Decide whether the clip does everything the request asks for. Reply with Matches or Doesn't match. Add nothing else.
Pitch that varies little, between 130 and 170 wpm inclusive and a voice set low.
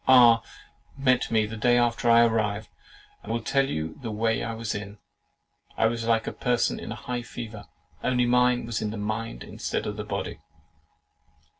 Doesn't match